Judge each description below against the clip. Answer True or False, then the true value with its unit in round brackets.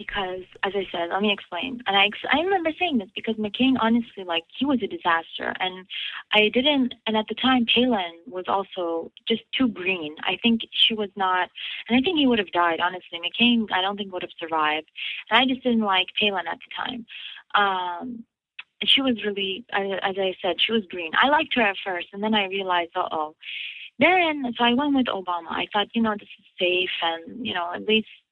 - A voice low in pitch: False (205 Hz)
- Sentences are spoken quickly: True (220 wpm)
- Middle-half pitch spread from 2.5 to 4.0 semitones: False (4.5 semitones)